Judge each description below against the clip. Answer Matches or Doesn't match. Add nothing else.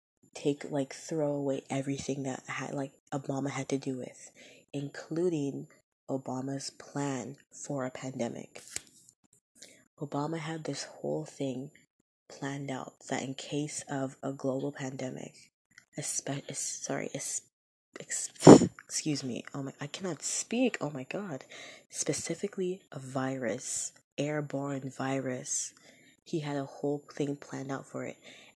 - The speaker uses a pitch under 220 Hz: Matches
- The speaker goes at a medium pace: Doesn't match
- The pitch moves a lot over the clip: Doesn't match